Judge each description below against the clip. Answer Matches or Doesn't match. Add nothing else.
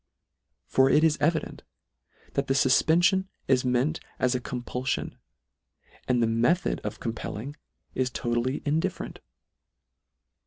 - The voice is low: Matches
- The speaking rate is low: Matches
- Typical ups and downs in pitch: Matches